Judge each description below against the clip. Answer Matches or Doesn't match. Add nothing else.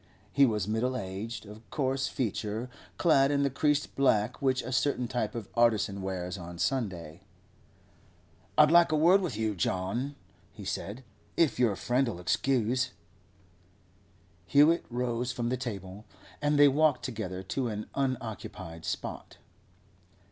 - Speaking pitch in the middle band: Doesn't match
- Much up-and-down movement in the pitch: Doesn't match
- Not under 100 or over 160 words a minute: Matches